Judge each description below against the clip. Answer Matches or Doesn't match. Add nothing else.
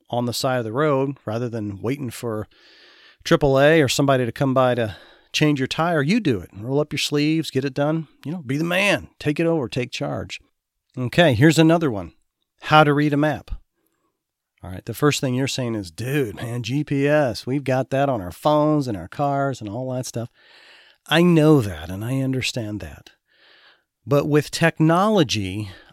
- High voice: Doesn't match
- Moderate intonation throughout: Matches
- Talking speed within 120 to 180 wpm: Doesn't match